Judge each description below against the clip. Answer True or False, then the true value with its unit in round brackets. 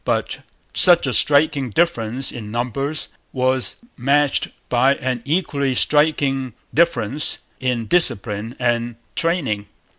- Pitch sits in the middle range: False (130 Hz)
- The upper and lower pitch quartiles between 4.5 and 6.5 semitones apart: False (3.6 semitones)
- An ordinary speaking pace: False (110 wpm)